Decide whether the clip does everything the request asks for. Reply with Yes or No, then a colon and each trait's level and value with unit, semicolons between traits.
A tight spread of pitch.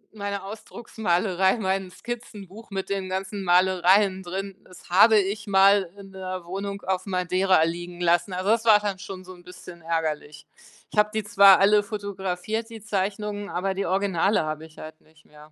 Yes: narrow, 2.1 semitones